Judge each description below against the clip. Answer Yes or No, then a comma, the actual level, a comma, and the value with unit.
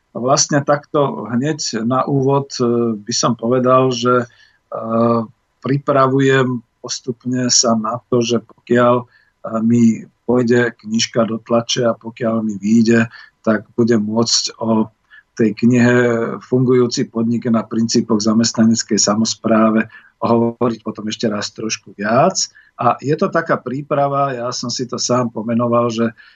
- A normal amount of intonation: No, narrow, 1.8 semitones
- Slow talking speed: No, average, 125 wpm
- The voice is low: Yes, low, 120 Hz